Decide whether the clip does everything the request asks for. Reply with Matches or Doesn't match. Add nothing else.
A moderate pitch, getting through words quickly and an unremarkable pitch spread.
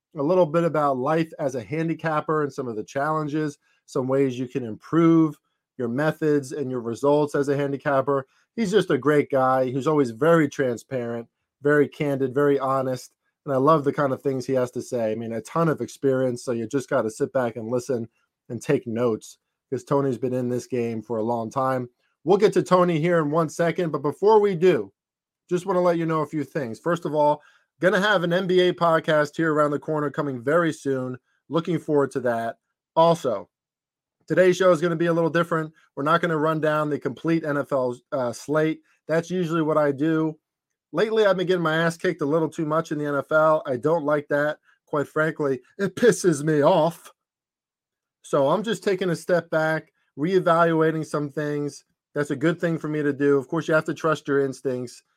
Matches